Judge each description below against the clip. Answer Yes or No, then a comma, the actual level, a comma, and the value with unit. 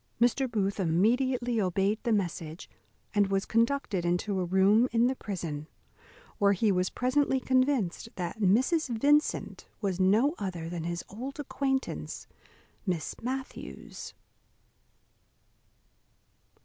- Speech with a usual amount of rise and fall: No, wide, 5.7 semitones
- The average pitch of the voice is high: Yes, high, 210 Hz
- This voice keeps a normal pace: No, slow, 115 wpm